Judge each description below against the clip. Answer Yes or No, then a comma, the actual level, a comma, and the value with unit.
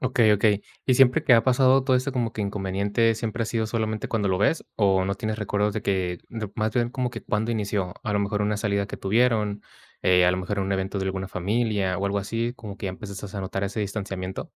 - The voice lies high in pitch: No, low, 105 Hz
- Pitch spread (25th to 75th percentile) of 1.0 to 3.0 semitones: Yes, narrow, 2.6 semitones